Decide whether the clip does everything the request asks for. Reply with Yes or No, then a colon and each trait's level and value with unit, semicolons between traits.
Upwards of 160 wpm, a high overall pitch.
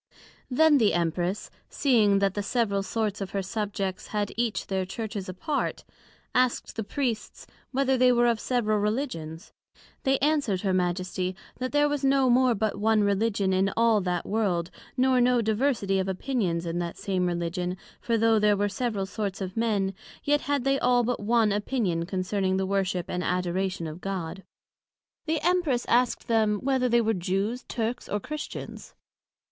Yes: average, 170 wpm; high, 210 Hz